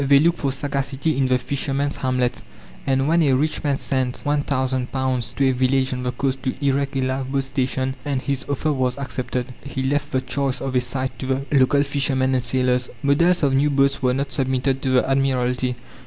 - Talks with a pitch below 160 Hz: Yes, low, 135 Hz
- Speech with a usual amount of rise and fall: No, narrow, 1.3 semitones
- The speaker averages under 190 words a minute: No, average, 200 wpm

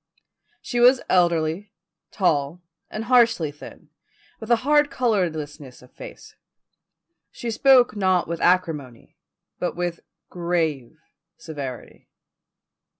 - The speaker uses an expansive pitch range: Yes, wide, 6.4 semitones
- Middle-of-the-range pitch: Yes, medium, 175 Hz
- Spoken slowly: Yes, slow, 100 wpm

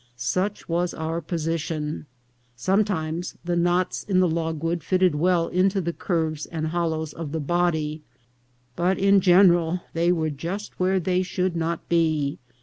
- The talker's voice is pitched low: No, medium, 170 Hz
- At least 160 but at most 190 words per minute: No, average, 145 wpm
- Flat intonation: Yes, narrow, 2.3 semitones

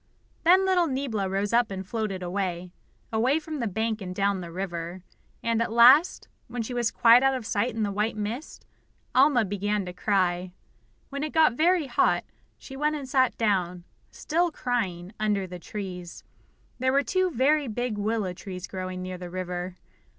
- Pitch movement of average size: No, wide, 5.7 semitones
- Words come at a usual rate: Yes, average, 180 wpm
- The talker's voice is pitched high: Yes, high, 215 Hz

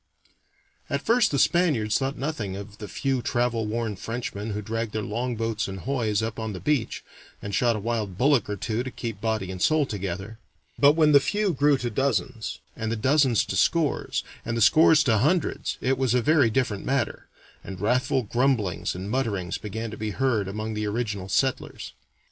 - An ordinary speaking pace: Yes, average, 195 wpm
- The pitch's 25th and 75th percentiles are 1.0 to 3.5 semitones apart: No, average, 4.2 semitones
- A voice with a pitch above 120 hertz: No, low, 115 Hz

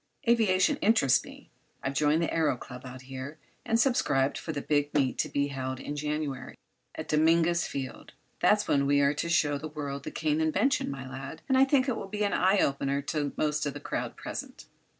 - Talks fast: Yes, fast, 210 wpm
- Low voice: No, medium, 150 Hz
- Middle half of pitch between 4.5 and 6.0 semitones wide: No, average, 3.5 semitones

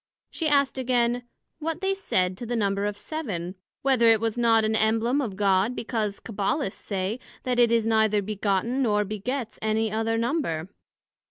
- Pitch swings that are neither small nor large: Yes, average, 3.3 semitones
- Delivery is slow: No, average, 170 wpm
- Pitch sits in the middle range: No, high, 225 Hz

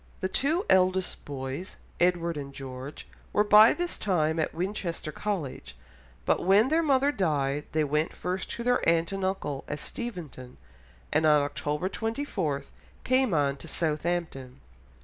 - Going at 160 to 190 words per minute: No, average, 150 wpm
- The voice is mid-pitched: Yes, medium, 170 Hz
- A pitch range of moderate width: No, wide, 5.9 semitones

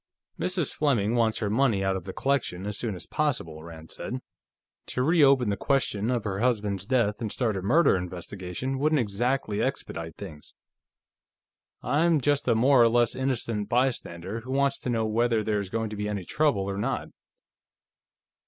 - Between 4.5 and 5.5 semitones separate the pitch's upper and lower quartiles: Yes, average, 4.9 semitones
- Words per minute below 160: No, average, 175 wpm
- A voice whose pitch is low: Yes, low, 115 Hz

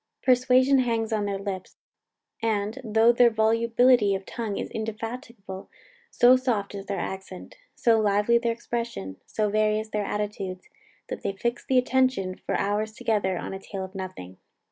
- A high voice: Yes, high, 215 Hz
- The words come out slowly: No, average, 160 wpm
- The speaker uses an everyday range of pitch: Yes, average, 3.1 semitones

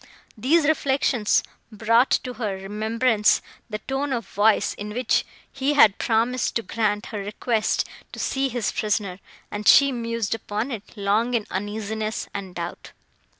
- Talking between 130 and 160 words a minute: Yes, average, 150 wpm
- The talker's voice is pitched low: No, high, 220 Hz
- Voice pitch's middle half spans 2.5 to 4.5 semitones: Yes, average, 3.1 semitones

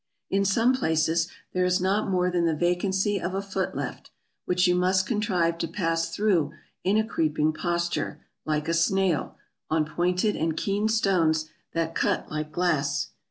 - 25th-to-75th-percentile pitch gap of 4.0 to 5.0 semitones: No, average, 3.1 semitones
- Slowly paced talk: No, average, 165 wpm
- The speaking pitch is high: No, medium, 180 Hz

